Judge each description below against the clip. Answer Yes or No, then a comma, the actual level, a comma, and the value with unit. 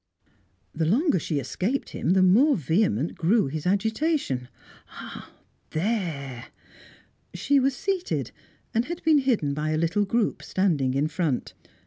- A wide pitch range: Yes, wide, 8.0 semitones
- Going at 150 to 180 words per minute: No, slow, 135 wpm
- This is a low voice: No, medium, 185 Hz